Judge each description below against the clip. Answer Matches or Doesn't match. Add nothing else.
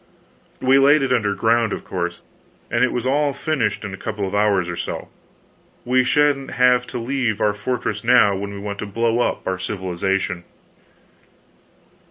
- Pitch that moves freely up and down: Doesn't match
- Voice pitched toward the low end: Matches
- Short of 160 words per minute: Doesn't match